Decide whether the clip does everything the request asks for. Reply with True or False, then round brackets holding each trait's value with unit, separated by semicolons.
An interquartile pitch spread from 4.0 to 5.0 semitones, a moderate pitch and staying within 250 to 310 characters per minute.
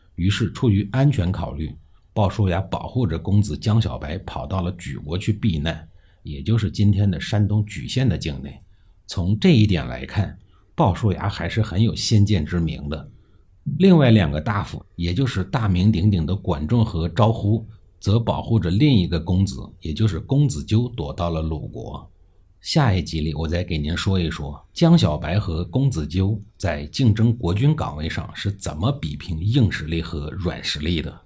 False (4.6 semitones; 95 Hz; 260 characters per minute)